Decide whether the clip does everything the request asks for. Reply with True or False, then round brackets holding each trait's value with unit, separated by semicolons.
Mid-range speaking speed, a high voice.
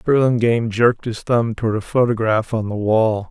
False (180 wpm; 115 Hz)